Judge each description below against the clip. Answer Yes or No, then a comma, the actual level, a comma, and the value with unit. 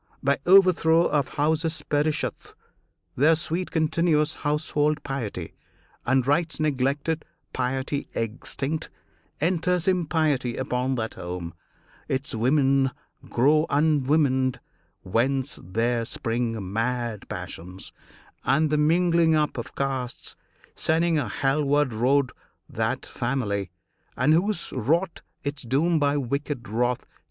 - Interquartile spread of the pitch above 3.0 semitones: Yes, average, 4.1 semitones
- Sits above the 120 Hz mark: Yes, medium, 140 Hz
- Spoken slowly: Yes, slow, 110 wpm